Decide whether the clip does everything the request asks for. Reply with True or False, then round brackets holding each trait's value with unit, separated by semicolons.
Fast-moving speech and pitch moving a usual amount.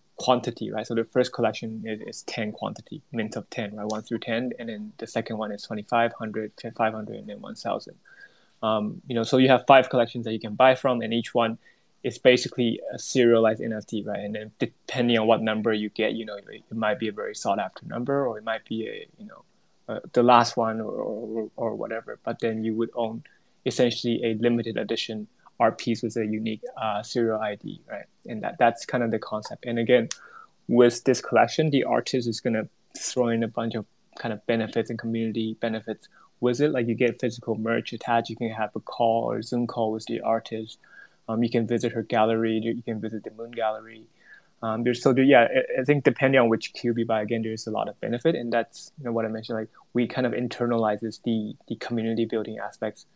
False (220 wpm; 1.5 semitones)